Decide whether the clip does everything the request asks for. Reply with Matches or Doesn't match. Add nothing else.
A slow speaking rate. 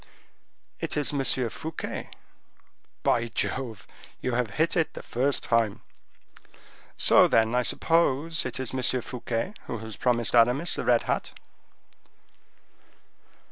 Matches